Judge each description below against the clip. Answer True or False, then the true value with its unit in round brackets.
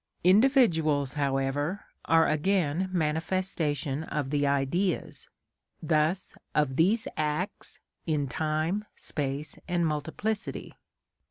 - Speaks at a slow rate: True (90 wpm)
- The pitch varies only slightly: False (4.1 semitones)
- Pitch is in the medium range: True (155 Hz)